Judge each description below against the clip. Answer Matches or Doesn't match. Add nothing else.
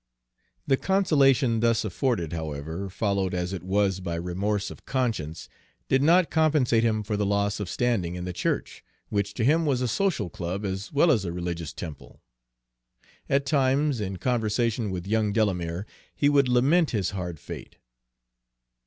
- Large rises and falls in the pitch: Matches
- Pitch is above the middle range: Doesn't match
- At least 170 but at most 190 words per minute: Doesn't match